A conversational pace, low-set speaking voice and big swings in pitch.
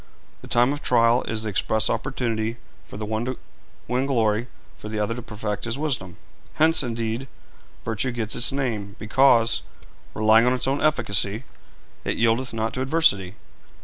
No: average, 165 wpm; low, 115 Hz; average, 2.9 semitones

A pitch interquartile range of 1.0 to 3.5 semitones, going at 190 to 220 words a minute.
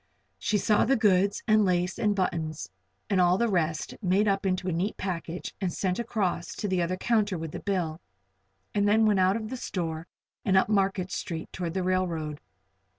Yes: average, 2.8 semitones; average, 195 wpm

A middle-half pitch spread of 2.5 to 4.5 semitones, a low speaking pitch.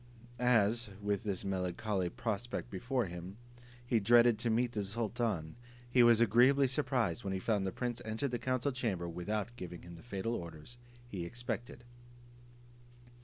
Yes: average, 4.0 semitones; low, 110 Hz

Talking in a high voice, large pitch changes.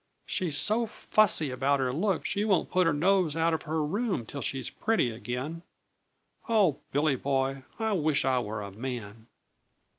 No: medium, 150 Hz; wide, 6.3 semitones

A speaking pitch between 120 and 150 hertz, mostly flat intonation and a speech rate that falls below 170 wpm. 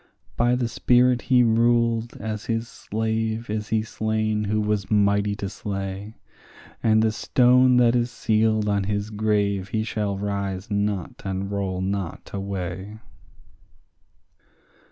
No: low, 105 Hz; narrow, 2.1 semitones; slow, 135 wpm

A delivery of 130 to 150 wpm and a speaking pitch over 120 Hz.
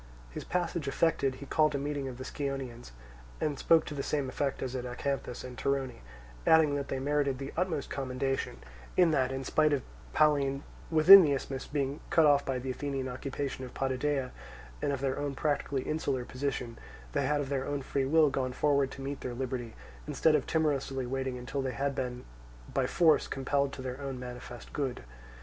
No: average, 195 wpm; low, 135 Hz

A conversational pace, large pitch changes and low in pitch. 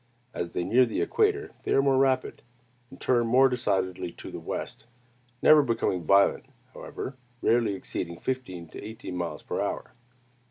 Yes: average, 160 wpm; wide, 6.1 semitones; low, 115 Hz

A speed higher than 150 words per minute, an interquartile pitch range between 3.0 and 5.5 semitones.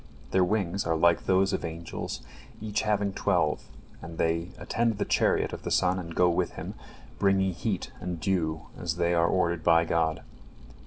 No: average, 175 wpm; narrow, 2.6 semitones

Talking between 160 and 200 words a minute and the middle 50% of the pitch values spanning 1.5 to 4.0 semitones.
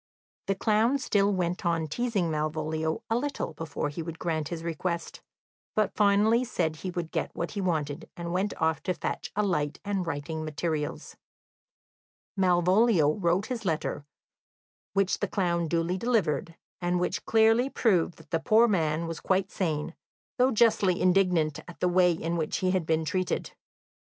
Yes: average, 165 wpm; average, 3.7 semitones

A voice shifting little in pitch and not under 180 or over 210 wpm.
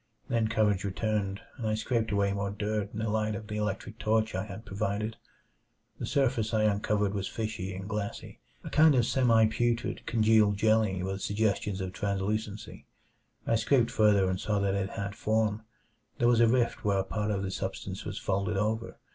Yes: narrow, 1.9 semitones; average, 190 wpm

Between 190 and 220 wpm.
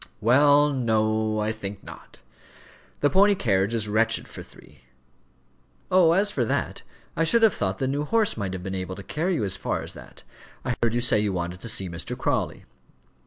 Yes: average, 200 wpm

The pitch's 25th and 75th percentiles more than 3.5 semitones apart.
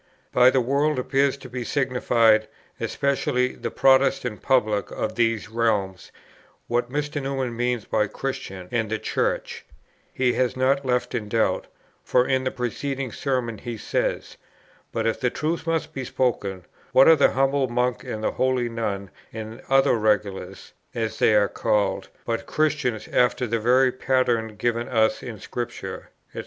No: average, 3.1 semitones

